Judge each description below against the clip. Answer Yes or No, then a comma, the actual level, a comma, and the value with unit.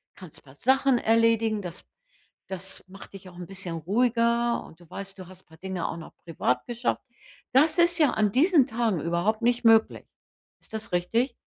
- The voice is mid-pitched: No, high, 215 Hz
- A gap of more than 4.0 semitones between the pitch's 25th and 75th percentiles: Yes, average, 5.0 semitones